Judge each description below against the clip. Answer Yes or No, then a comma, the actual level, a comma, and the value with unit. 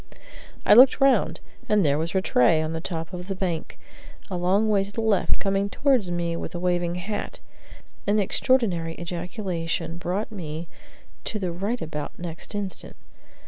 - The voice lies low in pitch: No, medium, 180 Hz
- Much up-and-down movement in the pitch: No, average, 3.4 semitones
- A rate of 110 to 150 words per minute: No, average, 165 wpm